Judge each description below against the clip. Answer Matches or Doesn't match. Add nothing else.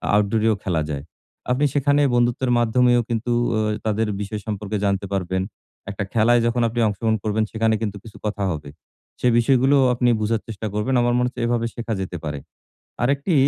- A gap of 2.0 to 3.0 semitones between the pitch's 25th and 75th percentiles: Matches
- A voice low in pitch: Matches